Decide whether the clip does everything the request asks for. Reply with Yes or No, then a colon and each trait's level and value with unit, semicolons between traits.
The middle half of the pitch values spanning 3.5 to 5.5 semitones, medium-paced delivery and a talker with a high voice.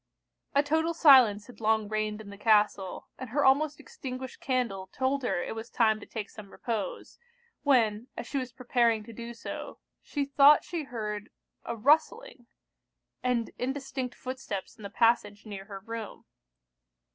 Yes: average, 3.9 semitones; average, 160 wpm; high, 235 Hz